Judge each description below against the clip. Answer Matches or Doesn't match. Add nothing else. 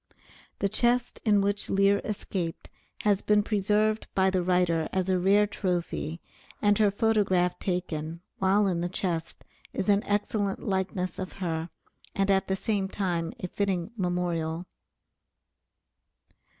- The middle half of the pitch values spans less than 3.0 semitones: Matches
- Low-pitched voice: Doesn't match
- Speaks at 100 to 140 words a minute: Matches